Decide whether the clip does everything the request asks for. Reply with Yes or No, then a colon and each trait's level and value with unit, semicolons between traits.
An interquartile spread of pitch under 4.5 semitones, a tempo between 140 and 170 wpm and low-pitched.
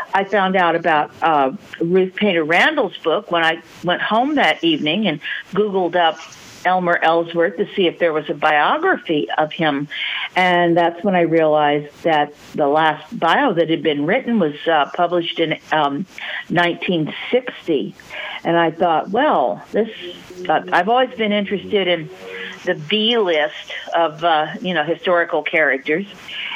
No: average, 3.3 semitones; average, 150 wpm; medium, 170 Hz